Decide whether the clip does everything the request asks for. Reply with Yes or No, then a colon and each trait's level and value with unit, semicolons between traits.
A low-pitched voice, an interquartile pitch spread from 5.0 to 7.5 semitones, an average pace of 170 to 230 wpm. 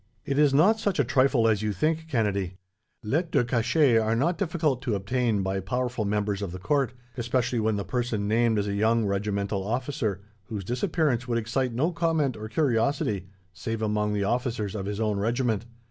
No: low, 115 Hz; average, 4.2 semitones; average, 190 wpm